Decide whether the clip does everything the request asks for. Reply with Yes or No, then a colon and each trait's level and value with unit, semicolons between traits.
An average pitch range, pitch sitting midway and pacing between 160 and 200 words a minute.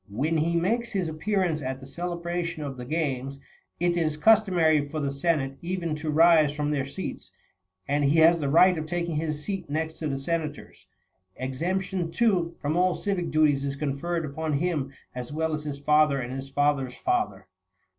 Yes: average, 3.4 semitones; medium, 155 Hz; average, 185 wpm